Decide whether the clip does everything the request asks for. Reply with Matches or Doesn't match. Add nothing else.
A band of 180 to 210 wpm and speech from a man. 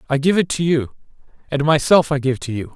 Doesn't match